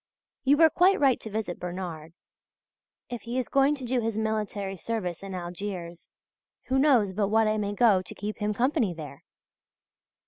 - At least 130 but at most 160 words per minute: No, average, 175 wpm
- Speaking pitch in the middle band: No, high, 215 Hz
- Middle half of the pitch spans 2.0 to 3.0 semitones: No, average, 4.8 semitones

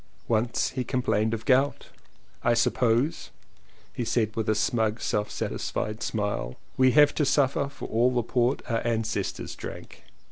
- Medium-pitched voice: No, low, 115 Hz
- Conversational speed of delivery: Yes, average, 150 wpm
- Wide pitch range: No, average, 2.7 semitones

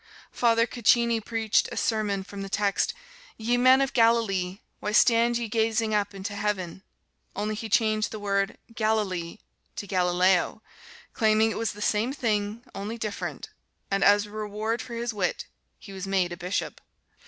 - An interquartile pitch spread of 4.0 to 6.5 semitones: No, narrow, 2.4 semitones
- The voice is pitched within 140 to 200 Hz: No, high, 215 Hz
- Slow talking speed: No, average, 160 wpm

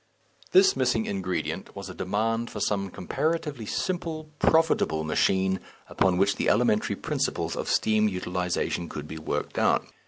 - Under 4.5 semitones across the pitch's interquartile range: No, average, 5.2 semitones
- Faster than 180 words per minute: No, average, 145 wpm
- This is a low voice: Yes, low, 100 Hz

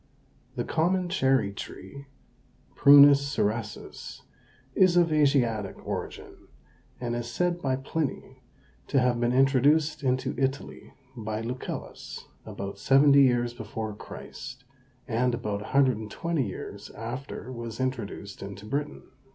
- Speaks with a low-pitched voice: Yes, low, 130 Hz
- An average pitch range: Yes, average, 3.8 semitones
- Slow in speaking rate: Yes, slow, 115 wpm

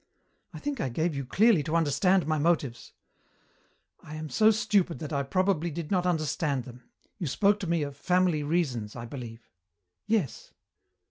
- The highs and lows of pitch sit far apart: No, average, 4.8 semitones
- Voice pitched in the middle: Yes, medium, 160 Hz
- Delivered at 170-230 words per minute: Yes, average, 175 wpm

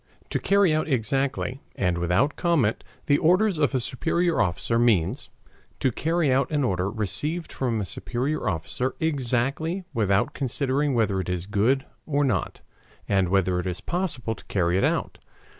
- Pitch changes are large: Yes, wide, 7.3 semitones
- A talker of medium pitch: No, low, 125 Hz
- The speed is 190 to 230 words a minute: No, average, 160 wpm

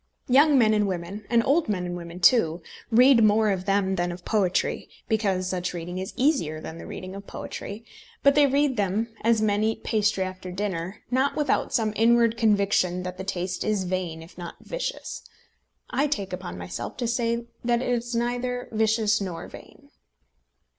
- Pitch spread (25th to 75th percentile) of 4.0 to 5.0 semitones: Yes, average, 4.4 semitones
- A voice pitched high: Yes, high, 210 Hz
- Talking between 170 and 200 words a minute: Yes, average, 180 wpm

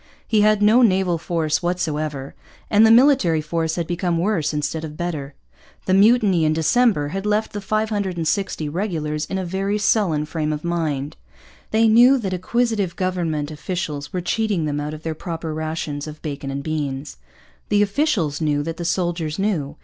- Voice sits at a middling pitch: Yes, medium, 170 Hz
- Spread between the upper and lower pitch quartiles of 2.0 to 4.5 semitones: No, average, 4.9 semitones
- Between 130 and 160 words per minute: No, average, 170 wpm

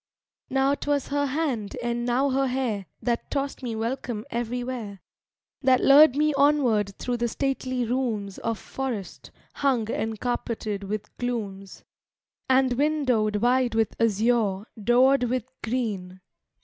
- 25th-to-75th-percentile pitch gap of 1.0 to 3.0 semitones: No, average, 3.5 semitones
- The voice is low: No, high, 245 Hz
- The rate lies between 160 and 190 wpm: No, slow, 135 wpm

